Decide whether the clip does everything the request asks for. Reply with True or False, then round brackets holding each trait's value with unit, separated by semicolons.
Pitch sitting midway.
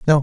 True (145 Hz)